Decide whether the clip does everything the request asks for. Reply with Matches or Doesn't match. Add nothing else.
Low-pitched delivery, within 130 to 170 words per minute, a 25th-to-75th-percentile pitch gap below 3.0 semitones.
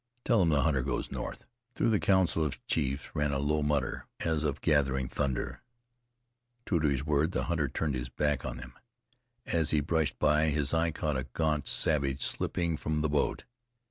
Doesn't match